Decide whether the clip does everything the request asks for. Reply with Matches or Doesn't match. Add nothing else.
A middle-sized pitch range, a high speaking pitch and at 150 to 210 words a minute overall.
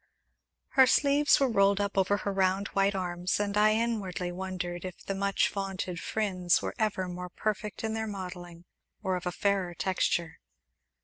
Doesn't match